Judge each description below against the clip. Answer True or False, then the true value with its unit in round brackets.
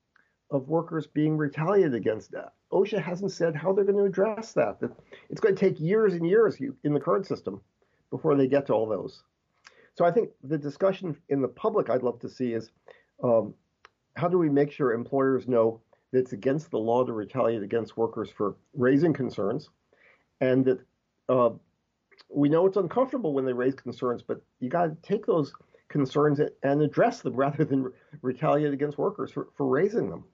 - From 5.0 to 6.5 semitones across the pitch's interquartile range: True (5.6 semitones)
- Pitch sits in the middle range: True (145 Hz)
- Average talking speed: True (190 wpm)